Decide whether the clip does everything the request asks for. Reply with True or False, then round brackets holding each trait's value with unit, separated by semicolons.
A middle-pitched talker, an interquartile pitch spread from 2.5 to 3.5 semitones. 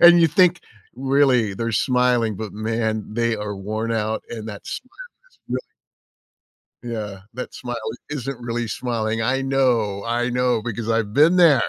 False (115 Hz; 2.9 semitones)